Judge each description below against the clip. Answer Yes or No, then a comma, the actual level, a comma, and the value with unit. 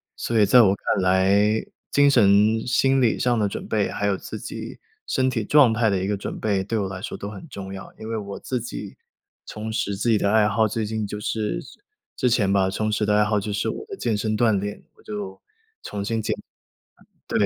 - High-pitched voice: No, low, 105 Hz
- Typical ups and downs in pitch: No, narrow, 2.0 semitones